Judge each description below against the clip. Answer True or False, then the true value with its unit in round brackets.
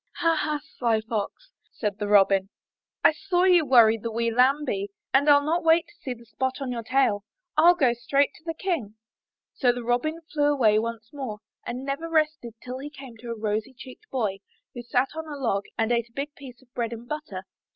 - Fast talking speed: True (215 wpm)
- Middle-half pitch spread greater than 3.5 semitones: True (4.7 semitones)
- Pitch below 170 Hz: False (255 Hz)